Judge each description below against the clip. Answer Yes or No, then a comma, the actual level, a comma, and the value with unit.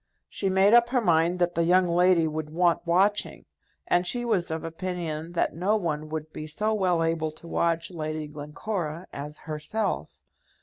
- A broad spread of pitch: No, average, 2.9 semitones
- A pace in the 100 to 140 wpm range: No, average, 175 wpm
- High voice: No, medium, 170 Hz